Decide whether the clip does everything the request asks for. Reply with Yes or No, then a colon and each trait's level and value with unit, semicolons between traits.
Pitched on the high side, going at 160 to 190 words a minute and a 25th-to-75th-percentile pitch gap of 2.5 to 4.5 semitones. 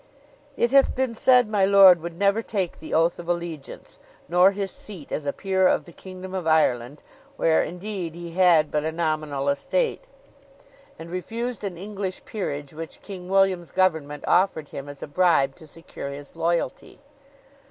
No: medium, 175 Hz; average, 170 wpm; average, 3.7 semitones